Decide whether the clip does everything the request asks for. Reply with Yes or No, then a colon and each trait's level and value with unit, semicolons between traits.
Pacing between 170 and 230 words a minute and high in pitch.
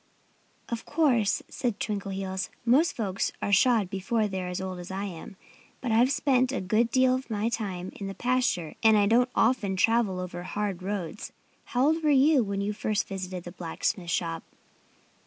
Yes: average, 180 wpm; high, 205 Hz